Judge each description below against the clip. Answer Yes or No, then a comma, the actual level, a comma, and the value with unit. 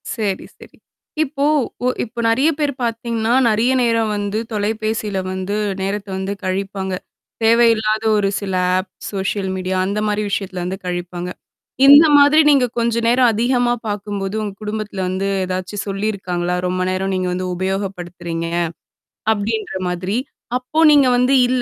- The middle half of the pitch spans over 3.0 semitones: Yes, average, 3.4 semitones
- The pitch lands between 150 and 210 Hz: Yes, high, 205 Hz